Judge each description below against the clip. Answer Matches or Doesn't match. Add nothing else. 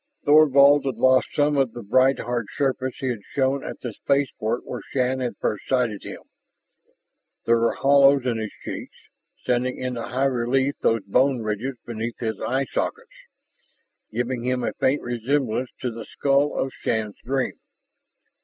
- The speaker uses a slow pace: Doesn't match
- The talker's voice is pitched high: Doesn't match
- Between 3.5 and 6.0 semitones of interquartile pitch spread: Doesn't match